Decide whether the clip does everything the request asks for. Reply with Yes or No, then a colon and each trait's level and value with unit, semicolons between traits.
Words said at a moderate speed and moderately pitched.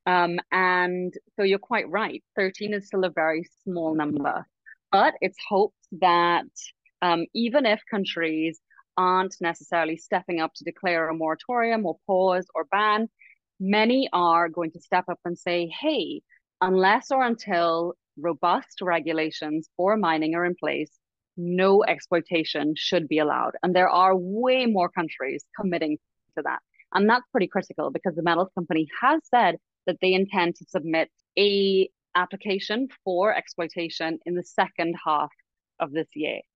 Yes: average, 150 wpm; medium, 180 Hz